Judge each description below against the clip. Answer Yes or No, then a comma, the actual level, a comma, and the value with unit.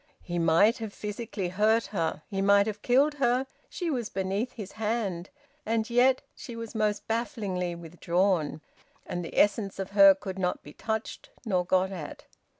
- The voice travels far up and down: No, average, 3.7 semitones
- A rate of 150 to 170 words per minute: Yes, average, 165 wpm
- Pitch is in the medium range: No, high, 200 Hz